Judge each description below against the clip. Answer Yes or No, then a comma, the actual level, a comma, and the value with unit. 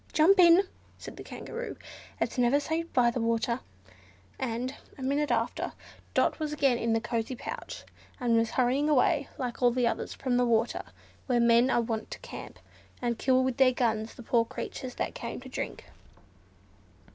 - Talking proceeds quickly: No, average, 180 wpm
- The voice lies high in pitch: Yes, very high, 250 Hz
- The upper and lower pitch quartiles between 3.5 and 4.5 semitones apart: No, average, 2.7 semitones